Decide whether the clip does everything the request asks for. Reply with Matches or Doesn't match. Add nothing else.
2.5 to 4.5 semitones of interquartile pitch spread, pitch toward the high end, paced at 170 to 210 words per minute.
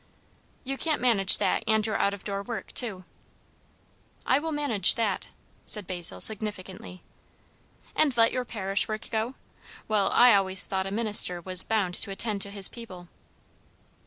Doesn't match